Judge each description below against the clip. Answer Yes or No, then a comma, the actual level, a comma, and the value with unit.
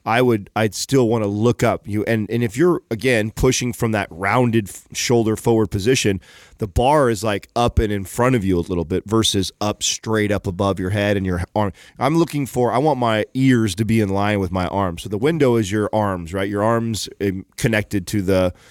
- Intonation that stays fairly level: No, average, 3.2 semitones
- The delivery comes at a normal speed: No, fast, 230 wpm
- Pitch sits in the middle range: No, low, 110 Hz